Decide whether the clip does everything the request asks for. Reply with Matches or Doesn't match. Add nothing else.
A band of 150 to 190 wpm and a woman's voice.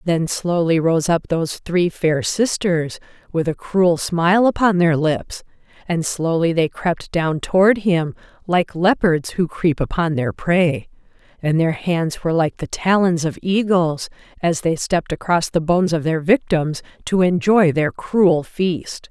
Matches